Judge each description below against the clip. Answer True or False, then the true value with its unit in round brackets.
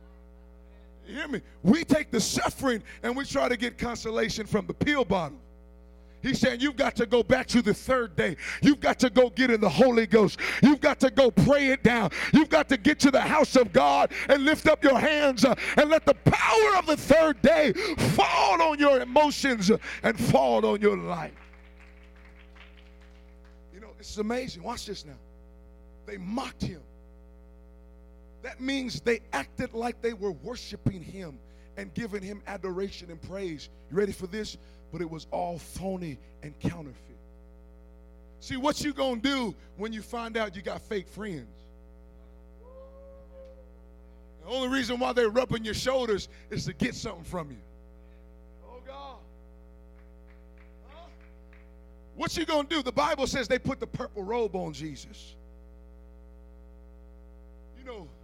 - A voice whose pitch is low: False (190 Hz)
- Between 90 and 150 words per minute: False (165 wpm)